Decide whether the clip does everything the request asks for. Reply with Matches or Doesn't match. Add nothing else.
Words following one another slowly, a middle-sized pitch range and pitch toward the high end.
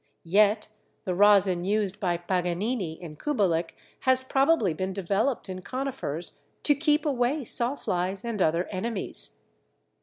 Doesn't match